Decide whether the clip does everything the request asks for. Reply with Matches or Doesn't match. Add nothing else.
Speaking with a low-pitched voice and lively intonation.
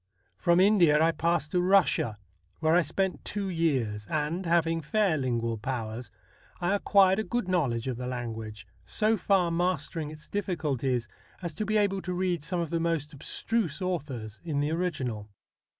Doesn't match